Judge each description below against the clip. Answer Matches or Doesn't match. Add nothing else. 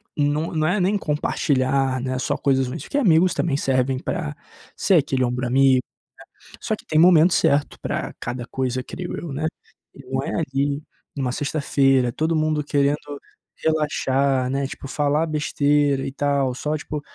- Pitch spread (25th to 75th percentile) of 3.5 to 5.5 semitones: Doesn't match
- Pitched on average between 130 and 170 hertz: Matches